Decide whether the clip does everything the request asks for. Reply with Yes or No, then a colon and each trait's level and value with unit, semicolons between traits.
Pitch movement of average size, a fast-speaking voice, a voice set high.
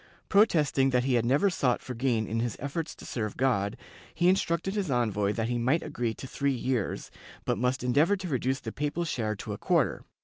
No: average, 4.5 semitones; fast, 210 wpm; low, 130 Hz